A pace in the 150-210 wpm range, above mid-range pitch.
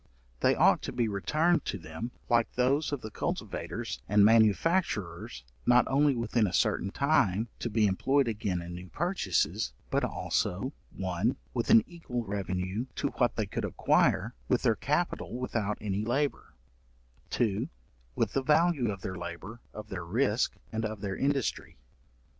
No: average, 160 wpm; low, 110 Hz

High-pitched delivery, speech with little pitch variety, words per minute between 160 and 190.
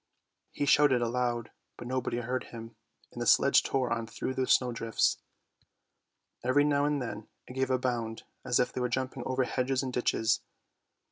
No: low, 125 Hz; narrow, 1.8 semitones; average, 175 wpm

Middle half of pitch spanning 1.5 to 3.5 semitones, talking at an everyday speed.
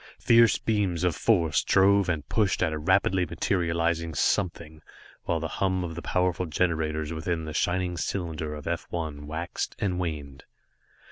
Yes: narrow, 2.6 semitones; average, 155 wpm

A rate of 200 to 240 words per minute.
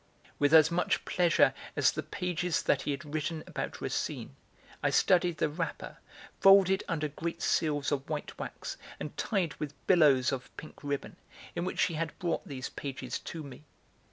No: average, 170 wpm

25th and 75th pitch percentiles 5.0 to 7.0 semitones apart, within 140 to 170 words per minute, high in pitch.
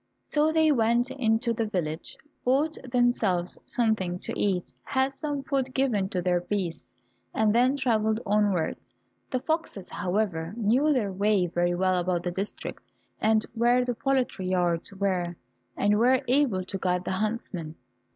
Yes: wide, 5.5 semitones; average, 150 wpm; high, 215 Hz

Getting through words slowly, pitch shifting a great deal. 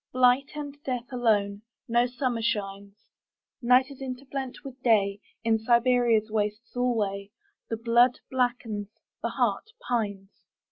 No: slow, 100 wpm; average, 3.0 semitones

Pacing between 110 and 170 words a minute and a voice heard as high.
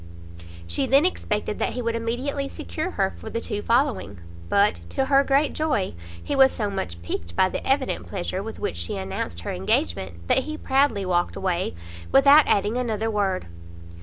No: average, 180 wpm; high, 210 Hz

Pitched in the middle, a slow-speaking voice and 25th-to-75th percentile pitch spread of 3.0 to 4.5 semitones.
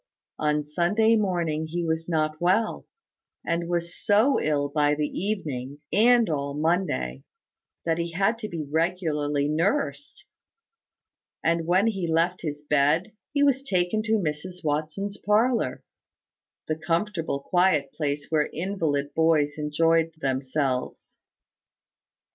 Yes: medium, 165 Hz; slow, 125 wpm; average, 4.2 semitones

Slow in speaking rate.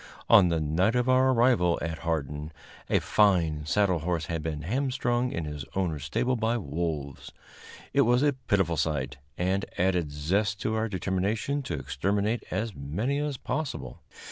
No: average, 160 wpm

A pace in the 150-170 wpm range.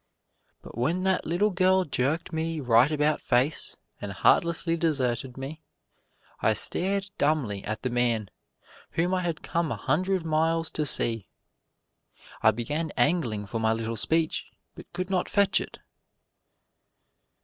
No: average, 140 wpm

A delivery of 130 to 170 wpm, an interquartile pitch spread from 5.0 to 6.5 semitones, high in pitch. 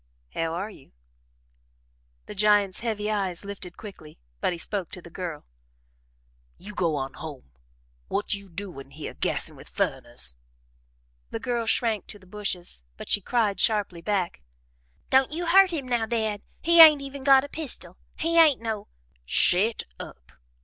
Yes: average, 160 wpm; average, 5.3 semitones; high, 205 Hz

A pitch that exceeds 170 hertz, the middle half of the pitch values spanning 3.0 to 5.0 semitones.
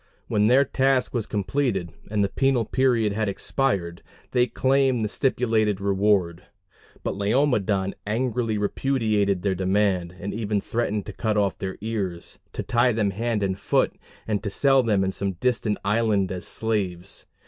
No: low, 105 Hz; average, 3.4 semitones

